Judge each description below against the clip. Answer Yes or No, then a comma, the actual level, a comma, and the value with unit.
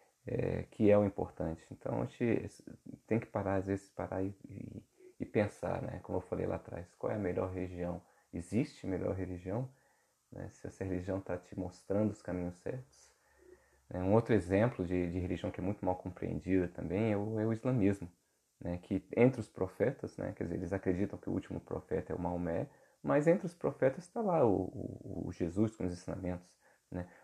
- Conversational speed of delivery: No, fast, 200 wpm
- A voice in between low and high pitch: No, very low, 95 Hz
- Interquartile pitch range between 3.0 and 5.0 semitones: Yes, average, 3.7 semitones